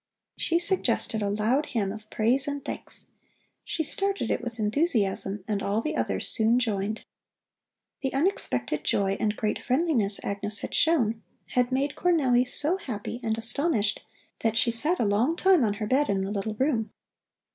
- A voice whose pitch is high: Yes, high, 230 Hz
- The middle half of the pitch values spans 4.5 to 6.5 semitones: Yes, wide, 5.5 semitones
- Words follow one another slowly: No, average, 170 wpm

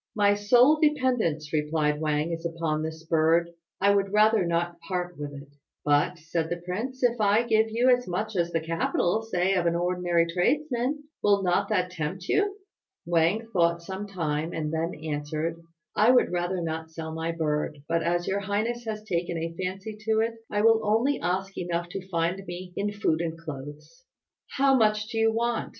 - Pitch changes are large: No, average, 4.6 semitones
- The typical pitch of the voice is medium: Yes, medium, 180 Hz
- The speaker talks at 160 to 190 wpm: Yes, average, 185 wpm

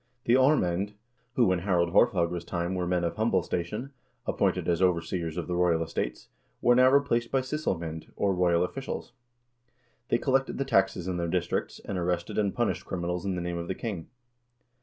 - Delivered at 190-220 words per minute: No, average, 180 wpm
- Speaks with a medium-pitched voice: No, very low, 90 Hz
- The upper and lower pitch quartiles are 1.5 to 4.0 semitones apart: No, average, 5.2 semitones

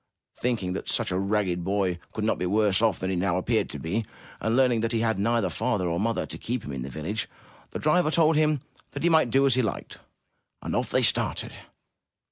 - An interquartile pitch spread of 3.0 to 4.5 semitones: No, average, 4.9 semitones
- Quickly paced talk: Yes, fast, 230 wpm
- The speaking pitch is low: Yes, low, 110 Hz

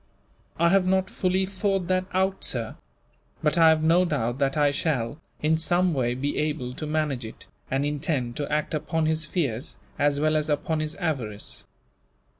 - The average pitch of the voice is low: No, medium, 155 Hz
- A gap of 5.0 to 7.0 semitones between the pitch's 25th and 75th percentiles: No, average, 3.6 semitones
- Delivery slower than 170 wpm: No, average, 180 wpm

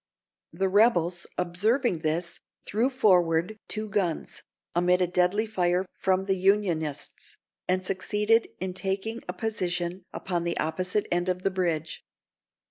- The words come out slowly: Yes, slow, 130 wpm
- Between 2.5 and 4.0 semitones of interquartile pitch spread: Yes, average, 2.9 semitones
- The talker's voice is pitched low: No, medium, 185 Hz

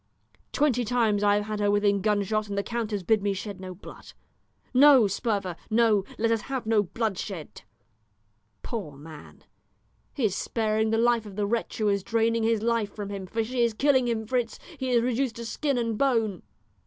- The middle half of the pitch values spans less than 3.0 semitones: Yes, narrow, 2.5 semitones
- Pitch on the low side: No, high, 220 Hz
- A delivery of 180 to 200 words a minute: Yes, average, 195 wpm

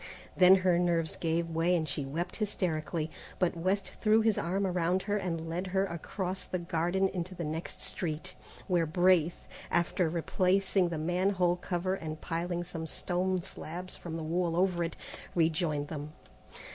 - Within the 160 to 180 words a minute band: Yes, average, 165 wpm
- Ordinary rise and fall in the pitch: No, narrow, 2.2 semitones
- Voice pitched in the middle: Yes, medium, 175 Hz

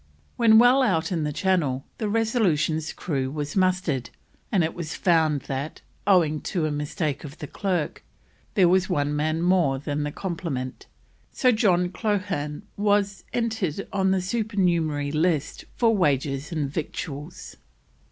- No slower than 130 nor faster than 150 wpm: Yes, average, 145 wpm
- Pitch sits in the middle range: Yes, medium, 170 Hz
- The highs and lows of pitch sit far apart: No, average, 4.7 semitones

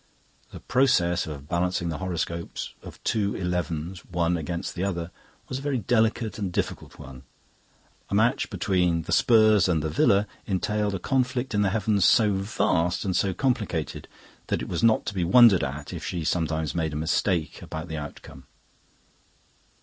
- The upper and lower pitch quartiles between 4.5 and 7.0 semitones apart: No, average, 4.1 semitones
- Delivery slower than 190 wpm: Yes, average, 170 wpm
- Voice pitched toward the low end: Yes, very low, 90 Hz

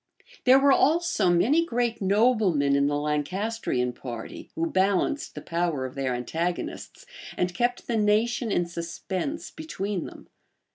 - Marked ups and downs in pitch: Yes, wide, 7.1 semitones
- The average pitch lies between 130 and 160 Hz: No, high, 190 Hz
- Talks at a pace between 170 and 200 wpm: No, average, 140 wpm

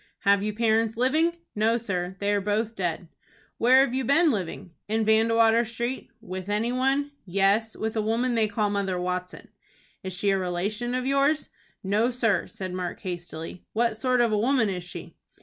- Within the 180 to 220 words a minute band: Yes, average, 185 wpm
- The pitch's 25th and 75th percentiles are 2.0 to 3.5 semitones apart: No, average, 3.9 semitones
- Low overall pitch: No, high, 220 Hz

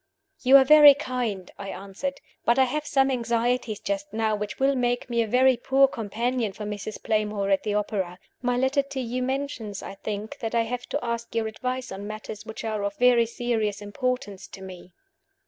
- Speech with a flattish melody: No, average, 3.5 semitones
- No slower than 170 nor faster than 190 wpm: No, average, 200 wpm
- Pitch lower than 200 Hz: No, high, 230 Hz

